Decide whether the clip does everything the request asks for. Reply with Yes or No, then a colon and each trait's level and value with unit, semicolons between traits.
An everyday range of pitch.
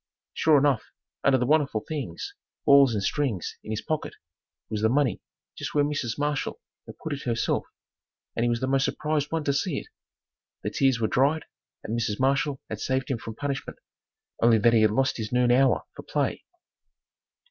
Yes: average, 3.9 semitones